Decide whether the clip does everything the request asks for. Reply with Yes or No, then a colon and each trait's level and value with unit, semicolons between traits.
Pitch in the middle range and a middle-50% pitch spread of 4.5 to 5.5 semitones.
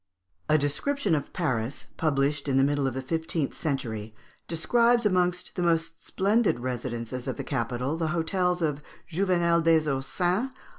Yes: medium, 160 Hz; average, 4.9 semitones